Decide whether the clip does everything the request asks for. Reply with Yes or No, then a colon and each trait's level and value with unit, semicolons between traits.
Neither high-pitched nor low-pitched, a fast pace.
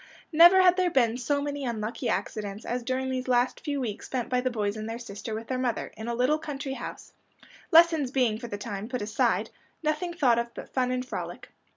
No: very high, 250 Hz; fast, 220 wpm